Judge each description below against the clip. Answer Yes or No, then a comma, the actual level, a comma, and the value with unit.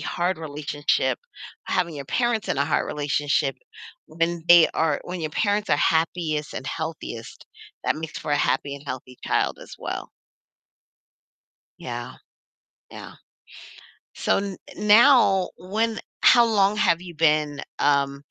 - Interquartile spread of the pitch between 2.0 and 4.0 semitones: No, average, 4.7 semitones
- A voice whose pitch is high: No, medium, 160 Hz